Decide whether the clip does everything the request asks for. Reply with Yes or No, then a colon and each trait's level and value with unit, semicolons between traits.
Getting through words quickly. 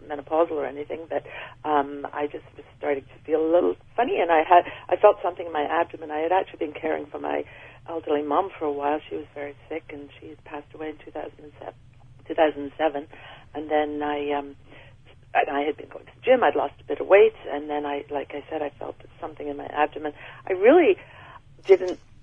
Yes: fast, 210 wpm